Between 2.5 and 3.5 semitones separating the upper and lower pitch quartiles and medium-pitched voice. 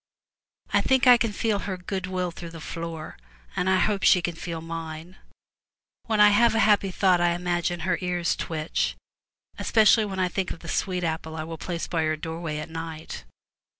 Yes: average, 2.9 semitones; medium, 175 Hz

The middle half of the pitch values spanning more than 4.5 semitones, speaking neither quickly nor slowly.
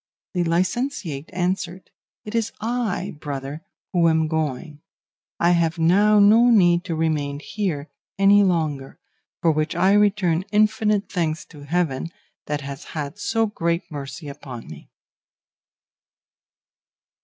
No: average, 5.0 semitones; slow, 125 wpm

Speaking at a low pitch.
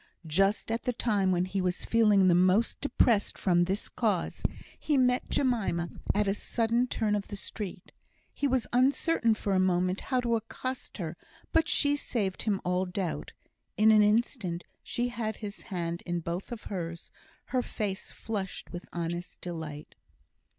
No: high, 205 Hz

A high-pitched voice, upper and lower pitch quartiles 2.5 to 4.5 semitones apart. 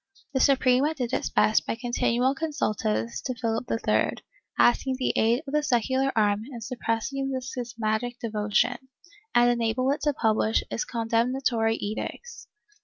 Yes: high, 240 Hz; average, 2.8 semitones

